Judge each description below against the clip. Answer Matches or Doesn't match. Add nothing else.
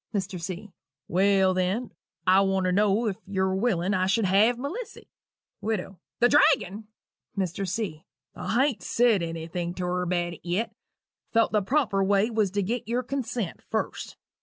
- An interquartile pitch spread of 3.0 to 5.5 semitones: Matches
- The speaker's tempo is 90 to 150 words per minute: Doesn't match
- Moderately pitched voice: Doesn't match